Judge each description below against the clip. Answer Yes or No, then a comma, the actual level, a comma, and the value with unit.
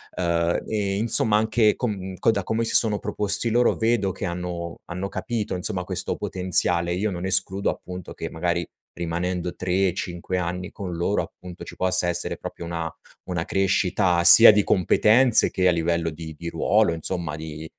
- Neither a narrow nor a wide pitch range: Yes, average, 3.0 semitones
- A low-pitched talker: Yes, very low, 90 Hz